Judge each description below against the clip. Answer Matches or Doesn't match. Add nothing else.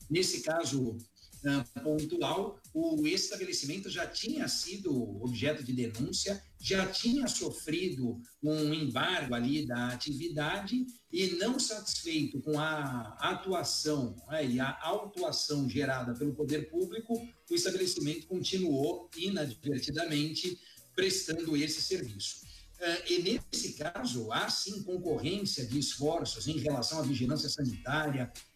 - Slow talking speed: Matches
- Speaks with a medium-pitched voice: Matches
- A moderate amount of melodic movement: Doesn't match